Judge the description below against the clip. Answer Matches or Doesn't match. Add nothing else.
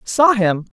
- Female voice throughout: Matches